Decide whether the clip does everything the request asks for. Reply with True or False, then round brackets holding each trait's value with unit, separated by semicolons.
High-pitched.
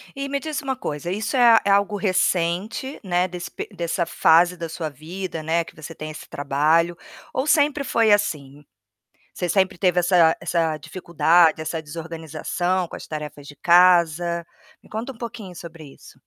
False (175 Hz)